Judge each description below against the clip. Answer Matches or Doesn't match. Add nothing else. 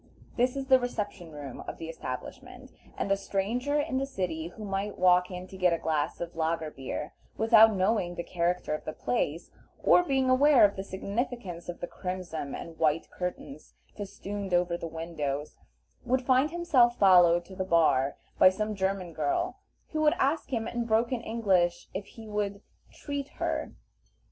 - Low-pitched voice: Doesn't match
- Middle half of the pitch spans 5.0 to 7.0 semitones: Matches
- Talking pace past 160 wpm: Matches